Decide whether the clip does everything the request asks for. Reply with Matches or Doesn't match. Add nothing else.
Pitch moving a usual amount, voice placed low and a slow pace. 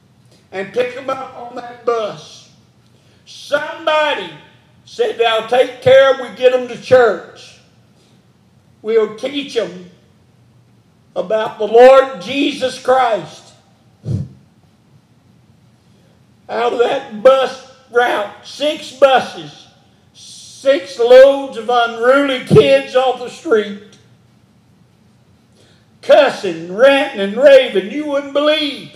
Doesn't match